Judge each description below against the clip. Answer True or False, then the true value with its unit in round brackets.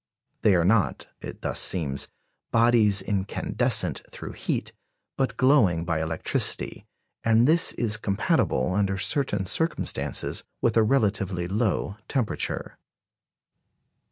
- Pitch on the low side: True (105 Hz)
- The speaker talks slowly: True (110 wpm)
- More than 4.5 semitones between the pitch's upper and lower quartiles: False (3.7 semitones)